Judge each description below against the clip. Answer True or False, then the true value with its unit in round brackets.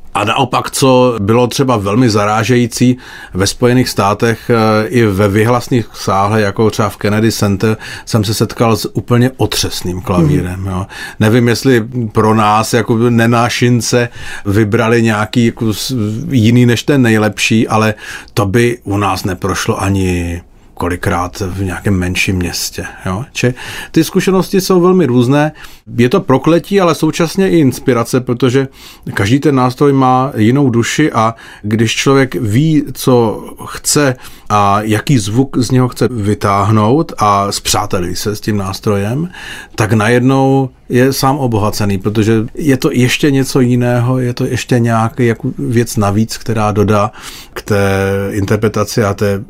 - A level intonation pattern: False (3.5 semitones)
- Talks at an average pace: True (140 wpm)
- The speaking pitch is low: True (115 Hz)